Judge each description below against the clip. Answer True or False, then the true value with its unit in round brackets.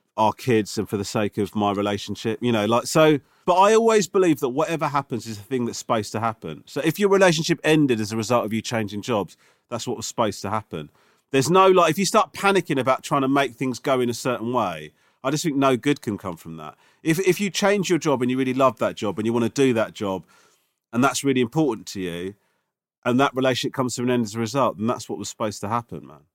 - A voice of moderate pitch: False (125 Hz)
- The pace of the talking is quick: True (260 wpm)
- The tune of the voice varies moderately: False (5.8 semitones)